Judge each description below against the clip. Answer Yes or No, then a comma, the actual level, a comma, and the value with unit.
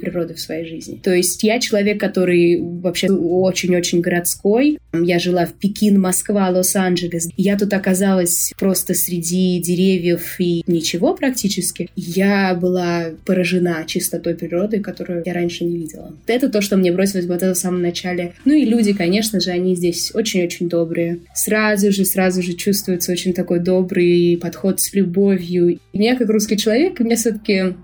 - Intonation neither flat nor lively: No, narrow, 2.3 semitones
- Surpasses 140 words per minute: Yes, fast, 160 wpm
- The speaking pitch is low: No, medium, 180 Hz